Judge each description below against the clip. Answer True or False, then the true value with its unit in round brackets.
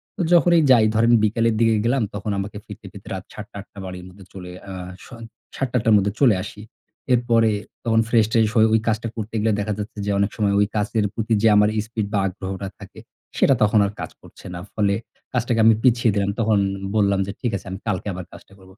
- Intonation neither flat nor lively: False (2.3 semitones)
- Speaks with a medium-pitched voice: False (110 Hz)